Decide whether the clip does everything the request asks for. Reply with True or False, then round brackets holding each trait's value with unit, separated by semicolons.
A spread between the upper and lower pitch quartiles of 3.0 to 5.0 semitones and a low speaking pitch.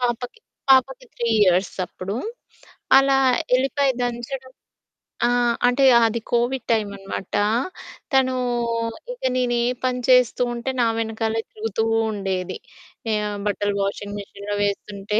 False (3.8 semitones; 230 Hz)